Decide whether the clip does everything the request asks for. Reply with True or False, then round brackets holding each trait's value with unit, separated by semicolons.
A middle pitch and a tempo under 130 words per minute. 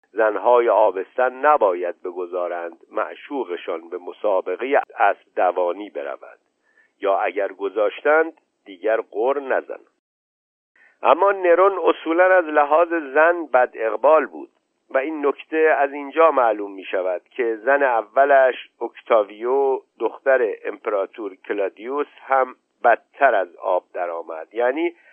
True (170 Hz; 110 wpm)